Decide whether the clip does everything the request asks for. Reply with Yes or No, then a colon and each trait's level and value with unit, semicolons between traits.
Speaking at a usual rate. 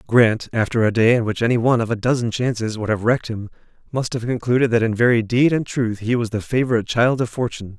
No: fast, 245 wpm